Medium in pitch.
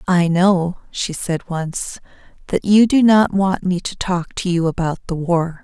Yes: medium, 180 Hz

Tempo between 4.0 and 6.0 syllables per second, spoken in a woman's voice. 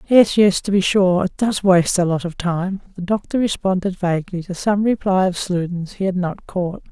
Yes: 5.0 syllables/s; female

